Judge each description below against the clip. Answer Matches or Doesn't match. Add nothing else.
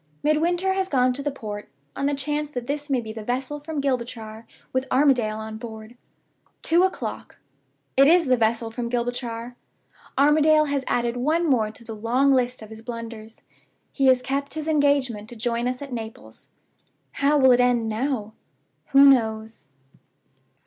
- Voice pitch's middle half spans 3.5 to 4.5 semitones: Matches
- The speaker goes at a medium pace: Matches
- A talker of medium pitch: Doesn't match